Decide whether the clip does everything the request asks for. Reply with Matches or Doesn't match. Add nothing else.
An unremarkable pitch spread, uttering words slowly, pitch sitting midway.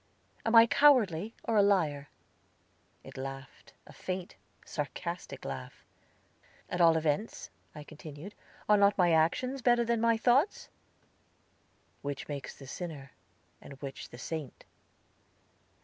Doesn't match